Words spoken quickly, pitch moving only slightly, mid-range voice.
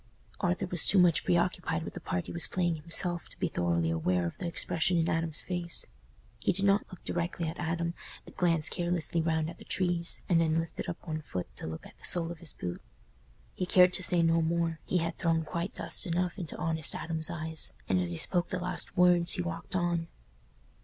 Yes: fast, 215 wpm; narrow, 1.7 semitones; medium, 170 Hz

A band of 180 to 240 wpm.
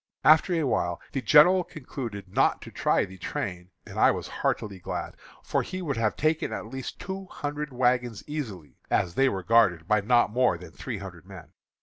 Yes: average, 195 wpm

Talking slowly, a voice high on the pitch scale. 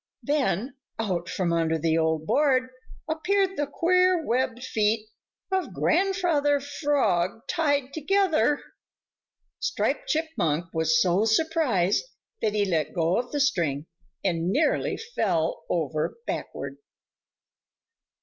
Yes: slow, 110 wpm; high, 245 Hz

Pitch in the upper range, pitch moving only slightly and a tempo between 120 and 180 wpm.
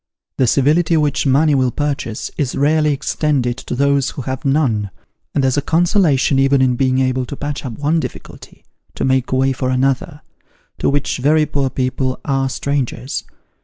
No: low, 135 Hz; narrow, 2.0 semitones; average, 170 wpm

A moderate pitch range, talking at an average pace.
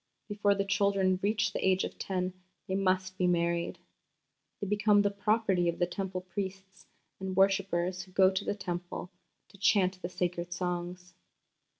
No: narrow, 1.8 semitones; average, 165 wpm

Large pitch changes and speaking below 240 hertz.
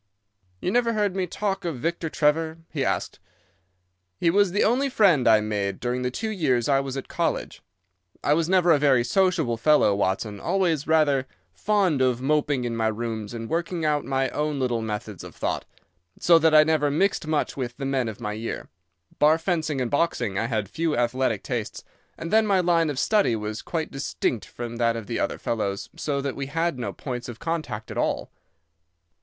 Yes: wide, 5.9 semitones; medium, 140 Hz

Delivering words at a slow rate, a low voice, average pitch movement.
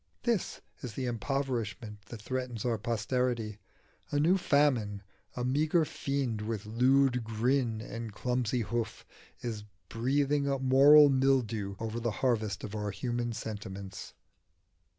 Yes: slow, 130 wpm; low, 120 Hz; average, 3.7 semitones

